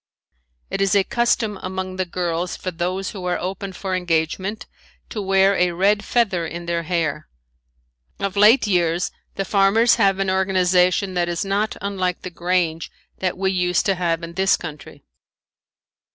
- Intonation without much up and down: Yes, narrow, 2.0 semitones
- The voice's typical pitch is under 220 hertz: Yes, medium, 185 Hz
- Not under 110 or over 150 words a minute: No, average, 165 wpm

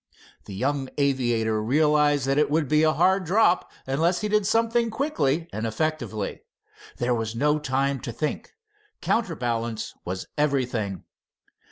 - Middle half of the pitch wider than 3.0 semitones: Yes, average, 5.1 semitones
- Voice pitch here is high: No, medium, 140 Hz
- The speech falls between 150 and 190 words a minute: No, average, 140 wpm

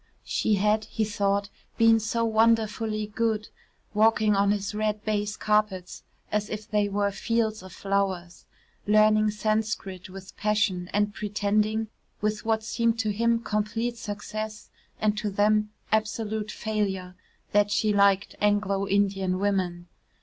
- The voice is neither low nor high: No, high, 210 Hz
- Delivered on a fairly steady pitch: Yes, narrow, 1.3 semitones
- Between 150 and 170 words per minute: No, slow, 135 wpm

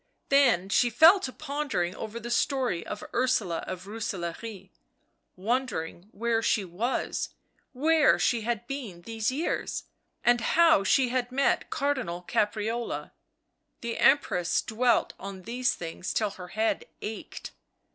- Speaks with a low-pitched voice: No, high, 230 Hz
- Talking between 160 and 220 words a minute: No, slow, 135 wpm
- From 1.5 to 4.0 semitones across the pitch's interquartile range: No, average, 4.9 semitones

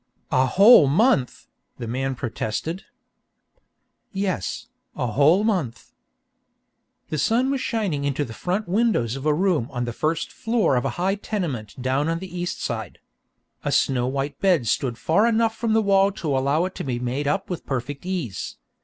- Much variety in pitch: Yes, wide, 7.1 semitones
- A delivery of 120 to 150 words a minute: No, average, 175 wpm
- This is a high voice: No, medium, 155 Hz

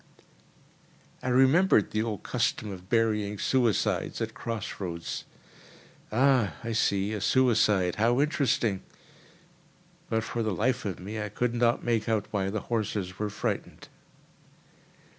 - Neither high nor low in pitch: No, low, 110 Hz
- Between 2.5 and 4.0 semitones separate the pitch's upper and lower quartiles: Yes, average, 3.0 semitones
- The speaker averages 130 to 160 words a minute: Yes, slow, 135 wpm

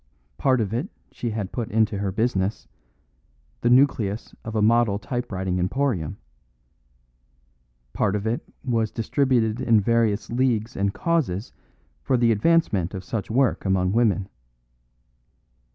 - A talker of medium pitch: No, low, 110 Hz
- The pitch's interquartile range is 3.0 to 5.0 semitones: Yes, average, 3.4 semitones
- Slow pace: Yes, slow, 130 wpm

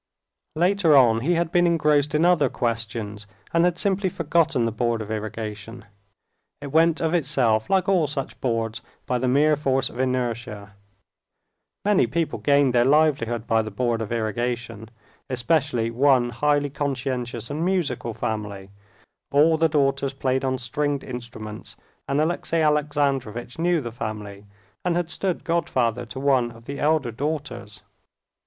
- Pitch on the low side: Yes, low, 130 Hz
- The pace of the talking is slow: No, average, 150 wpm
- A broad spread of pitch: No, average, 4.8 semitones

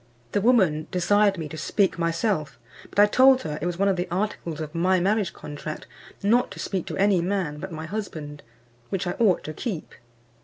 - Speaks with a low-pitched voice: No, medium, 185 Hz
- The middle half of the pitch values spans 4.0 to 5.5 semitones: Yes, average, 4.3 semitones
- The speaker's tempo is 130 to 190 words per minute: No, average, 200 wpm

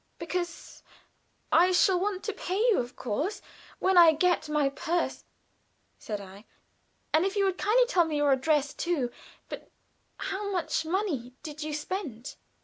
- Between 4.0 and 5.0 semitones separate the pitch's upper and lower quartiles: Yes, average, 4.6 semitones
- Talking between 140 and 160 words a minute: Yes, average, 155 wpm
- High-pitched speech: Yes, very high, 335 Hz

